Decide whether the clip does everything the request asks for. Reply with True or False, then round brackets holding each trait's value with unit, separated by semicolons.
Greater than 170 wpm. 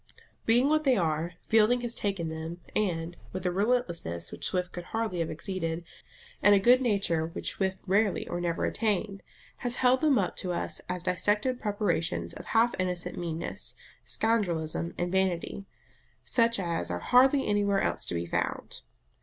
False (165 wpm)